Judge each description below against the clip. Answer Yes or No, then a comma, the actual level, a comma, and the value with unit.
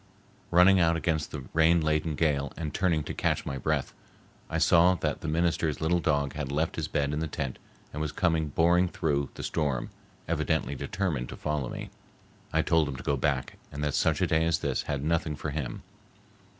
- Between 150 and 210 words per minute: Yes, average, 200 wpm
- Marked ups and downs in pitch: No, narrow, 2.4 semitones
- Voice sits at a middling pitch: No, very low, 80 Hz